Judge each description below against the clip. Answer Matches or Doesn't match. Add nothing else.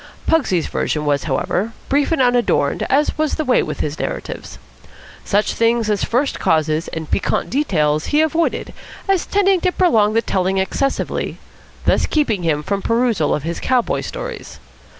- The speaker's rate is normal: Matches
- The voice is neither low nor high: Doesn't match